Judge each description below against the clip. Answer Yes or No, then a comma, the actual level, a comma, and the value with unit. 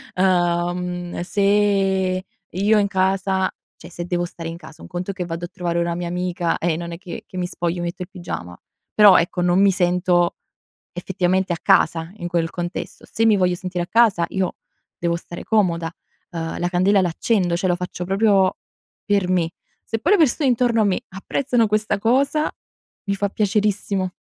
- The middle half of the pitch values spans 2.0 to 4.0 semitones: Yes, narrow, 2.5 semitones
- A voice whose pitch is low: No, medium, 185 Hz